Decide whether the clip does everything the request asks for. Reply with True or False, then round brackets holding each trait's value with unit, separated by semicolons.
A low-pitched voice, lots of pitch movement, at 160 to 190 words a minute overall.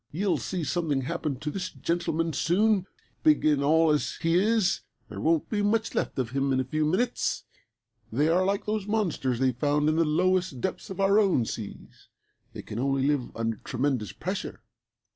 False (160 Hz; 5.7 semitones; 185 wpm)